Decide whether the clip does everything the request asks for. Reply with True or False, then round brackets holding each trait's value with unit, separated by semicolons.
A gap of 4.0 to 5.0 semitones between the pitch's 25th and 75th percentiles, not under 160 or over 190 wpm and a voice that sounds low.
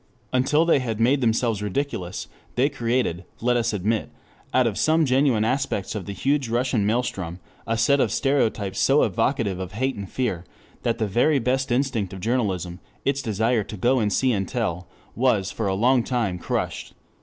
True (4.4 semitones; 180 wpm; 115 Hz)